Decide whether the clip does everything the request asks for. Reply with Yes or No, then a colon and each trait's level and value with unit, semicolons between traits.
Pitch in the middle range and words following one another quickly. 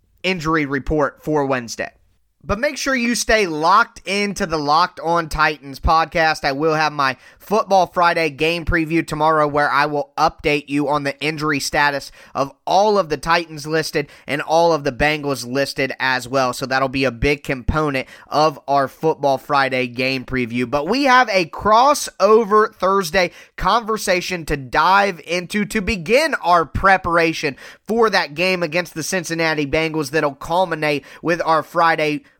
No: medium, 155 Hz; average, 160 wpm